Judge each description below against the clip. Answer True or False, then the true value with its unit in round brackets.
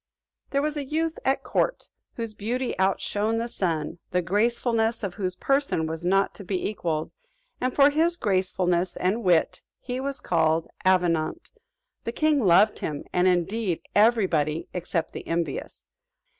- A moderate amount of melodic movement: False (5.7 semitones)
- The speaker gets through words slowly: False (155 wpm)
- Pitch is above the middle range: True (200 Hz)